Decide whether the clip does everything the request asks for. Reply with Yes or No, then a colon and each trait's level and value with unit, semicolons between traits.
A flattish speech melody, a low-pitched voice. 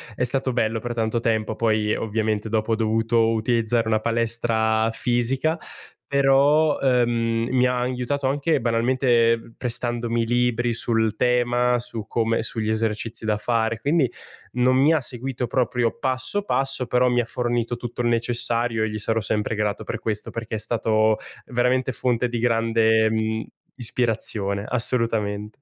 Yes: narrow, 1.9 semitones; low, 115 Hz